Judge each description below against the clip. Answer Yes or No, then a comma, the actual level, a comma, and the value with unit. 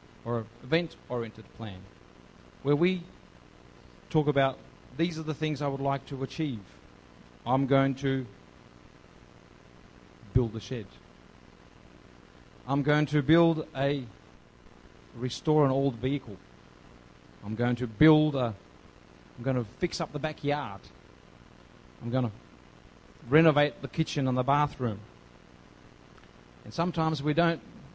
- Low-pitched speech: Yes, low, 110 Hz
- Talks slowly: Yes, slow, 120 wpm